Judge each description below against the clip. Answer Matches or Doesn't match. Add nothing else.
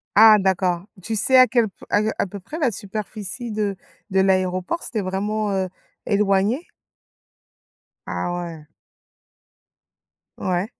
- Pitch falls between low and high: Doesn't match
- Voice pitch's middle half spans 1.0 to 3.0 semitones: Matches